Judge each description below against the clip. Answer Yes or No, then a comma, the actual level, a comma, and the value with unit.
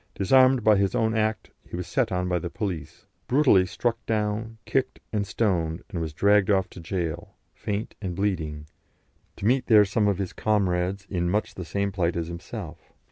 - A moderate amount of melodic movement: Yes, average, 3.6 semitones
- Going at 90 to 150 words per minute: No, average, 190 wpm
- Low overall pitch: Yes, low, 100 Hz